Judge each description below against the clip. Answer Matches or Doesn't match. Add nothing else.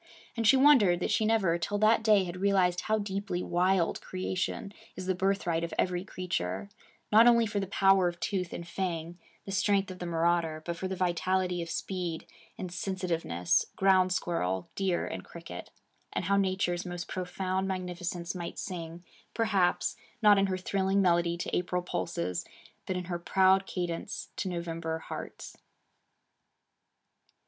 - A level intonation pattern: Matches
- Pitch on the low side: Doesn't match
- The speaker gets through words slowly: Doesn't match